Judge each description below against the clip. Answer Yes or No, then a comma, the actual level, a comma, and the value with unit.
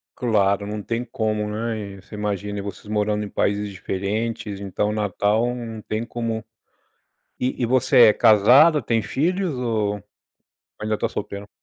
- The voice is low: Yes, low, 110 Hz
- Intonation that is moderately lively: No, narrow, 2.3 semitones